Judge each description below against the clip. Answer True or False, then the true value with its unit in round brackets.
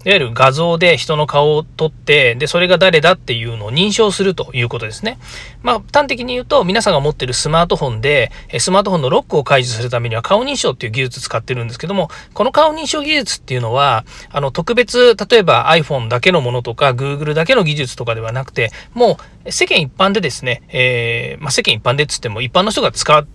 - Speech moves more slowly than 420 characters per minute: False (470 characters per minute)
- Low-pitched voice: False (150 Hz)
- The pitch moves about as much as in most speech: False (7.0 semitones)